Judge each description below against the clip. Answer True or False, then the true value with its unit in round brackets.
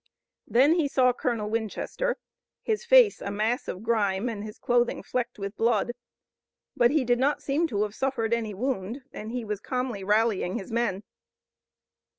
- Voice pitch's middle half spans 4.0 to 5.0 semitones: False (3.5 semitones)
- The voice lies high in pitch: True (235 Hz)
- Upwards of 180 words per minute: False (165 wpm)